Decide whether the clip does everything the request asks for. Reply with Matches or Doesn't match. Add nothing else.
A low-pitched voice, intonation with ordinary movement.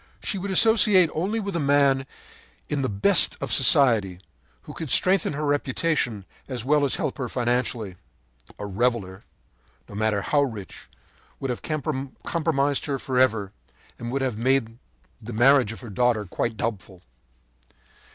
Matches